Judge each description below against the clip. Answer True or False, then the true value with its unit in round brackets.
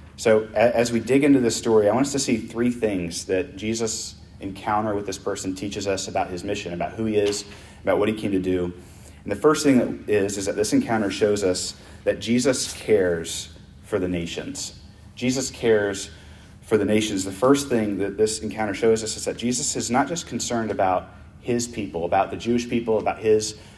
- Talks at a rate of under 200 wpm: False (205 wpm)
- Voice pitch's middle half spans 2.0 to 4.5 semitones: True (3.0 semitones)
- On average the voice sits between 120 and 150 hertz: False (105 Hz)